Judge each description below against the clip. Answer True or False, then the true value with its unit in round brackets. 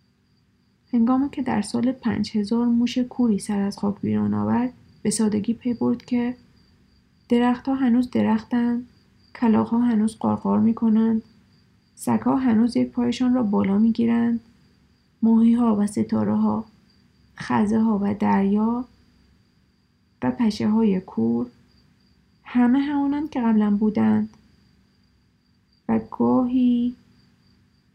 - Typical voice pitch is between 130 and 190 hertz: False (230 Hz)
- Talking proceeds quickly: False (120 wpm)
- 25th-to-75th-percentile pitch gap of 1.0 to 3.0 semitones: True (2.6 semitones)